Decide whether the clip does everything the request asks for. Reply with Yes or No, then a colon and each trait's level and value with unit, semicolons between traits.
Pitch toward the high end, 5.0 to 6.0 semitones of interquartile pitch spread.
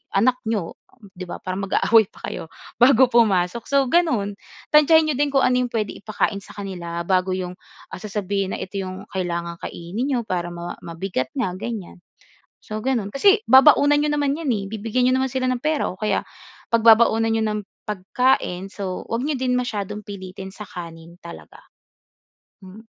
Yes: high, 210 Hz; average, 5.3 semitones